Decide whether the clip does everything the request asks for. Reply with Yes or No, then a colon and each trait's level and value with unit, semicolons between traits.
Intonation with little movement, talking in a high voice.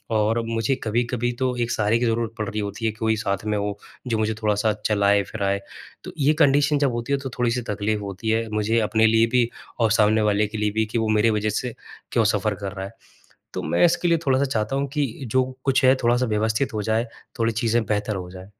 No: narrow, 2.3 semitones; low, 110 Hz